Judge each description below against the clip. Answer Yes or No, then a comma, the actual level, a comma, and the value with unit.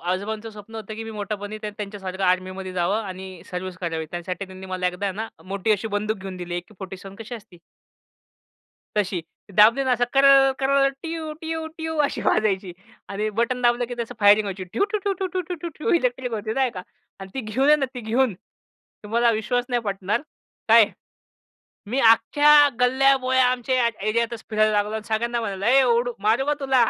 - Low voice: No, high, 220 Hz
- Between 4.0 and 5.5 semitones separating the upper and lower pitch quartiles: Yes, average, 4.9 semitones